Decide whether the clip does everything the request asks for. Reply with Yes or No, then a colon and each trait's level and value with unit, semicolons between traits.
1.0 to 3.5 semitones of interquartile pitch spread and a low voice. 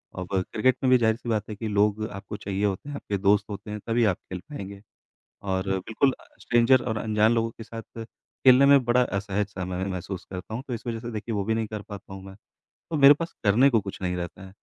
Yes: average, 3.1 semitones; low, 105 Hz